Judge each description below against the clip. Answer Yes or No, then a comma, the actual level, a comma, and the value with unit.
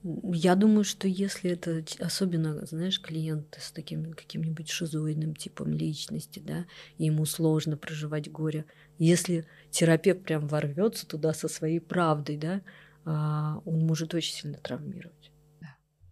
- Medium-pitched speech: Yes, medium, 160 Hz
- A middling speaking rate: Yes, average, 125 wpm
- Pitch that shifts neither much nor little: No, narrow, 2.2 semitones